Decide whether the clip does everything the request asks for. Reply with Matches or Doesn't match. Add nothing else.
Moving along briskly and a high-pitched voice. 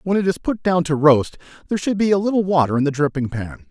Doesn't match